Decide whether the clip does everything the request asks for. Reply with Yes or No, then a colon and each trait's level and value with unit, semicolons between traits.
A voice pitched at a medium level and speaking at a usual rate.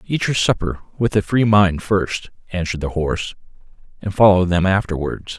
No: very low, 95 Hz; average, 165 wpm